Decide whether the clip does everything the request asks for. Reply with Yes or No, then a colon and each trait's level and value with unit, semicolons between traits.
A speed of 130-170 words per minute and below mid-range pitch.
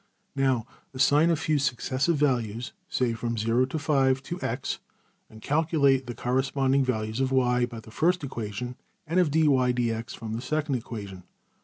Yes: average, 140 wpm; low, 130 Hz